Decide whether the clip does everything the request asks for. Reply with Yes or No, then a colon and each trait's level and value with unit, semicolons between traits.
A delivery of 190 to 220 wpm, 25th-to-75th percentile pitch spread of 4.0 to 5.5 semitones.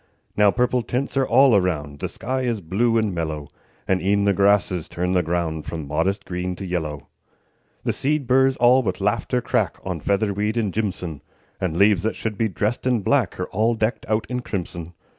Yes: average, 195 wpm; average, 4.9 semitones